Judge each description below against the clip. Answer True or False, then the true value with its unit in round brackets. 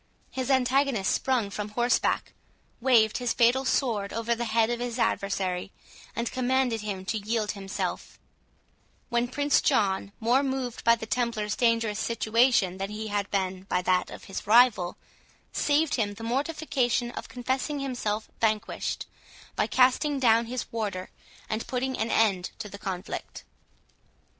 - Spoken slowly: False (150 wpm)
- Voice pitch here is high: True (230 Hz)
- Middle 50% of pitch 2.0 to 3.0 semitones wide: False (3.5 semitones)